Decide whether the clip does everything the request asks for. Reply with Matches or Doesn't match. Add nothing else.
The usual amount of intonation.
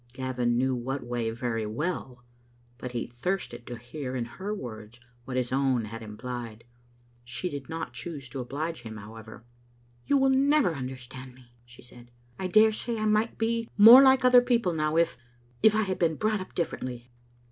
Doesn't match